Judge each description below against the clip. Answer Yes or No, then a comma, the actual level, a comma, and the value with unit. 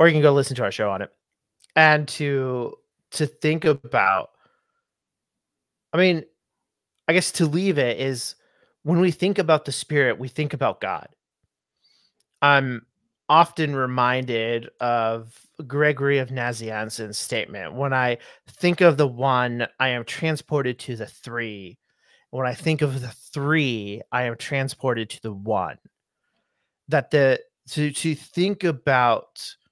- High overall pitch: No, medium, 140 Hz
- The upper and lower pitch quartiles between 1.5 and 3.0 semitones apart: No, average, 4.2 semitones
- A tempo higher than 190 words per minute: No, average, 145 wpm